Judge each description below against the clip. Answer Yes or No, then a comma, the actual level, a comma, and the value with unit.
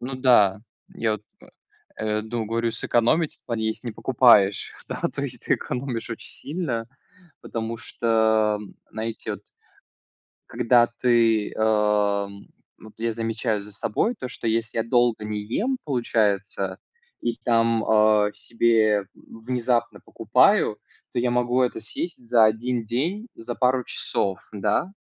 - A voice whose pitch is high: No, low, 115 Hz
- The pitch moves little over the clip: Yes, narrow, 2.2 semitones